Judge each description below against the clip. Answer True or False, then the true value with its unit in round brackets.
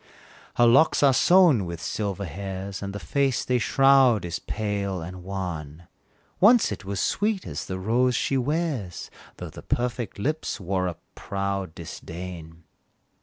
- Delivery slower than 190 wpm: True (150 wpm)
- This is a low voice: True (100 Hz)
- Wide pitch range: True (5.7 semitones)